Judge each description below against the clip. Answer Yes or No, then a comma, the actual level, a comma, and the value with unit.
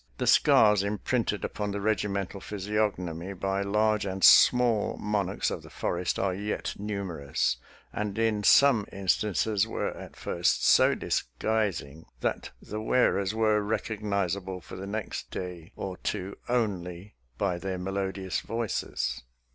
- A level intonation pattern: Yes, narrow, 2.2 semitones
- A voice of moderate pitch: No, low, 100 Hz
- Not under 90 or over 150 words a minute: Yes, average, 140 wpm